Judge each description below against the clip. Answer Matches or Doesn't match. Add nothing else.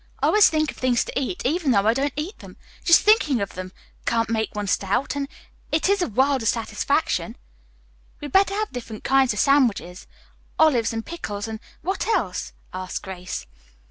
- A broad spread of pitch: Matches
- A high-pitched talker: Matches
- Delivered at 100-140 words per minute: Doesn't match